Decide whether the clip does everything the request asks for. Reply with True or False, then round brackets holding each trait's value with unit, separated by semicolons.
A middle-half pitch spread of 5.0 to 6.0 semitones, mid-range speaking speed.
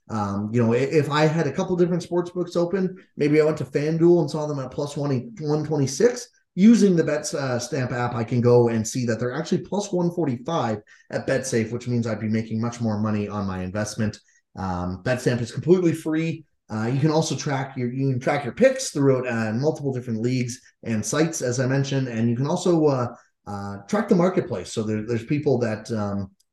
False (5.6 semitones; 215 wpm)